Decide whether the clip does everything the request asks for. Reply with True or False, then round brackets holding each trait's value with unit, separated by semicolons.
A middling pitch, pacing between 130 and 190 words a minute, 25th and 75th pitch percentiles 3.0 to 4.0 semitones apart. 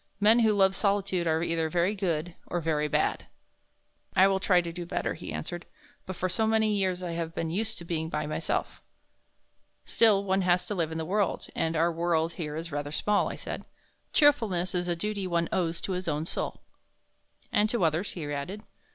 False (175 Hz; 205 wpm; 3.3 semitones)